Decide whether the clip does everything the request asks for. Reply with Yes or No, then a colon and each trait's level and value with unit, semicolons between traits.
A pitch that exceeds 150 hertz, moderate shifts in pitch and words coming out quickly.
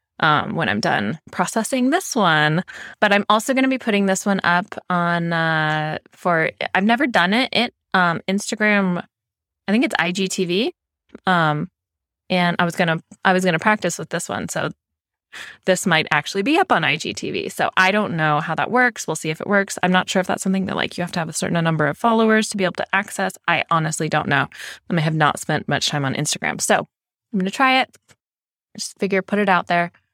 Yes: medium, 185 Hz; average, 4.5 semitones; fast, 215 wpm